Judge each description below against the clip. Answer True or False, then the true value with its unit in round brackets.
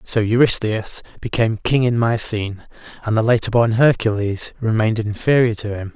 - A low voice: True (110 Hz)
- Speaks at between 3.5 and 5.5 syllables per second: True (5.4 syllables/s)